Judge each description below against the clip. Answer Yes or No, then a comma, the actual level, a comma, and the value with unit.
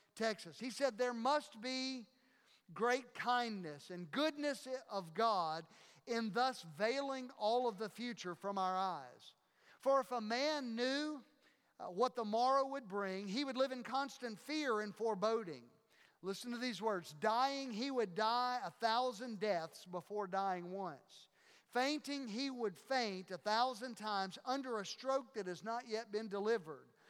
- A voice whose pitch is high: Yes, high, 230 Hz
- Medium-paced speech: Yes, average, 155 wpm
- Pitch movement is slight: No, average, 4.1 semitones